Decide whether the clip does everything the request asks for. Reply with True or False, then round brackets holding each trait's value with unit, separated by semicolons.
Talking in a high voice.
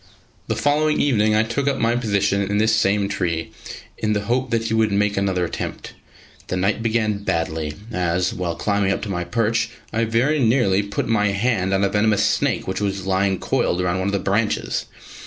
False (105 Hz)